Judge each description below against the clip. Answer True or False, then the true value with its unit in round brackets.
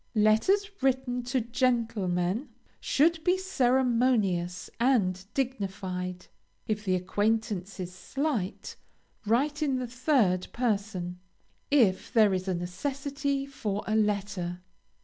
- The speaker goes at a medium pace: False (110 wpm)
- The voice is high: True (220 Hz)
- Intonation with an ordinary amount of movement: False (5.9 semitones)